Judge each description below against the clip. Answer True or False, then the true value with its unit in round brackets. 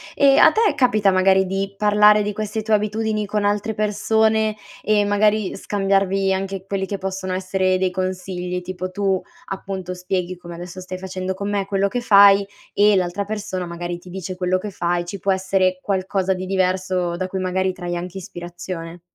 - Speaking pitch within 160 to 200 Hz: True (190 Hz)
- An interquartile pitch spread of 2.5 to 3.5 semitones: False (1.8 semitones)